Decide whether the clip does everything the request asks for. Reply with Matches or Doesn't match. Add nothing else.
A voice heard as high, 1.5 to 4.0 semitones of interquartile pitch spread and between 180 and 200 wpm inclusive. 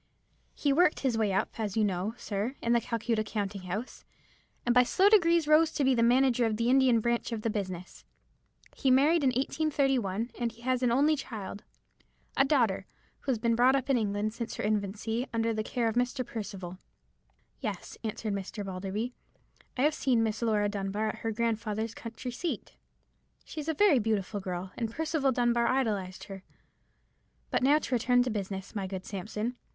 Matches